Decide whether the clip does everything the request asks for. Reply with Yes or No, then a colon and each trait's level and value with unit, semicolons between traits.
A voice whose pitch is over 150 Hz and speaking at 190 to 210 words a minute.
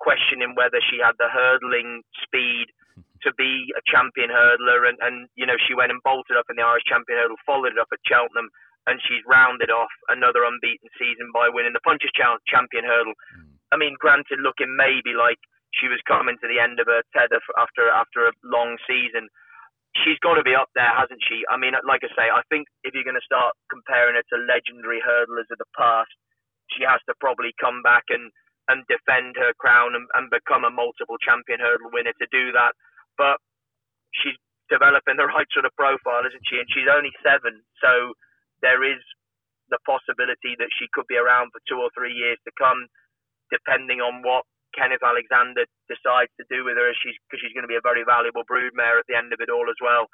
No: low, 125 Hz; fast, 205 wpm